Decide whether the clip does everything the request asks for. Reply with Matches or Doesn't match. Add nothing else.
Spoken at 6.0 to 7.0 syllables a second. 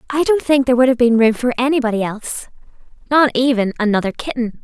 Matches